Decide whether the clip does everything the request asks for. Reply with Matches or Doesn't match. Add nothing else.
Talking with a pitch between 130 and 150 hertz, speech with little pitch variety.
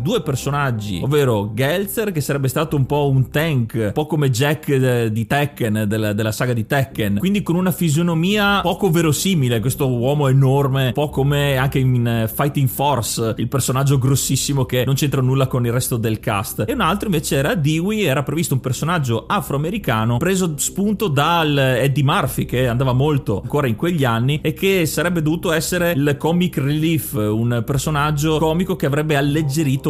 Doesn't match